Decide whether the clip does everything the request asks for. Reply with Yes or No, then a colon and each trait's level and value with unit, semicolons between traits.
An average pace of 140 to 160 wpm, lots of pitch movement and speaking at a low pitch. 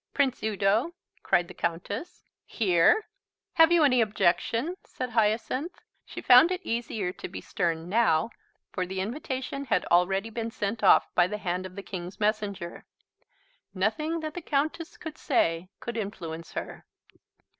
No: average, 150 wpm; wide, 6.5 semitones; high, 215 Hz